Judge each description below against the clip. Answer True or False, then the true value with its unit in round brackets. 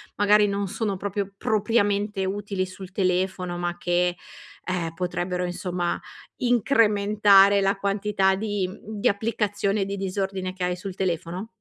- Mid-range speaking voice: False (195 Hz)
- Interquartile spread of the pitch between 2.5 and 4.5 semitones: False (2.0 semitones)